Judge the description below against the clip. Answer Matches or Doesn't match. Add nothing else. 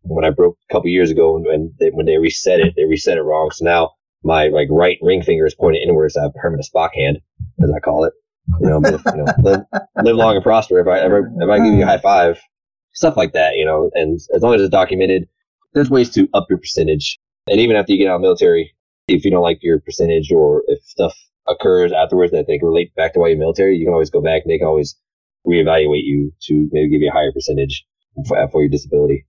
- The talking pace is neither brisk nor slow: Doesn't match